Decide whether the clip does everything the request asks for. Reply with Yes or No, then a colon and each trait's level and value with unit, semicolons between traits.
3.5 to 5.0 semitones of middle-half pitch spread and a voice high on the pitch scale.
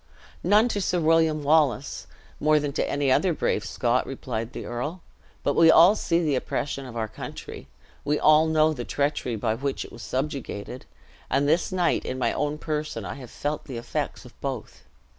No: average, 4.1 semitones; medium, 145 Hz